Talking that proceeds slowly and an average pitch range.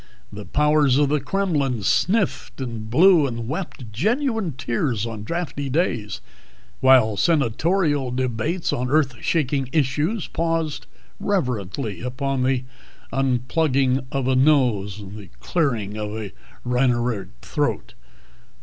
Yes: slow, 115 wpm; average, 4.7 semitones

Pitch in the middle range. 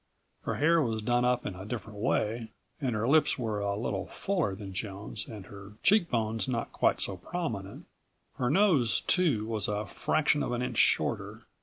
No: low, 115 Hz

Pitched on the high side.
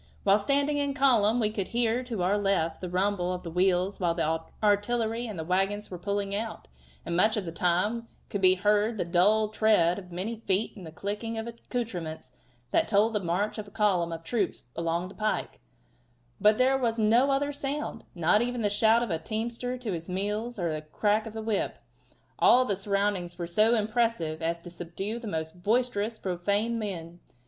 Yes: high, 205 Hz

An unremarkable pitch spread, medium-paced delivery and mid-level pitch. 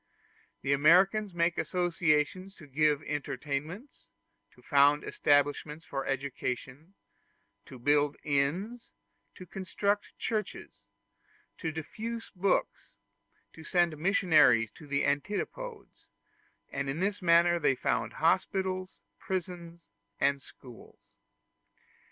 No: average, 4.7 semitones; slow, 100 wpm; medium, 160 Hz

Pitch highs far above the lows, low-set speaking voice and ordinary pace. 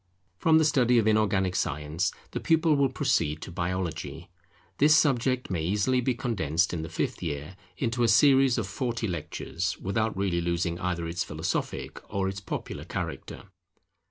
Yes: wide, 6.5 semitones; low, 100 Hz; average, 160 wpm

